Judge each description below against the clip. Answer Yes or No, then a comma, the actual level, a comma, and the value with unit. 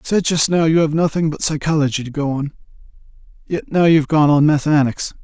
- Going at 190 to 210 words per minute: Yes, fast, 205 wpm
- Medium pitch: Yes, medium, 155 Hz